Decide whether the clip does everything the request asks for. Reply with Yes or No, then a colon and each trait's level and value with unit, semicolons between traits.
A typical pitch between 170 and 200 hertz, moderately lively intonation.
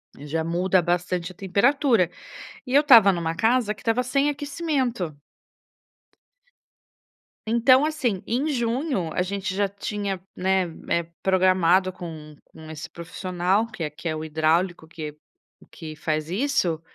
No: medium, 185 Hz; wide, 6.0 semitones